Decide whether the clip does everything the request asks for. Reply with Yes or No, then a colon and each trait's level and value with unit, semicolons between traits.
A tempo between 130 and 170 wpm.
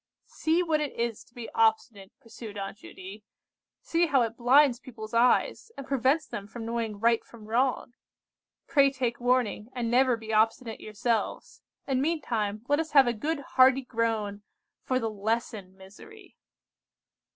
Yes: average, 155 wpm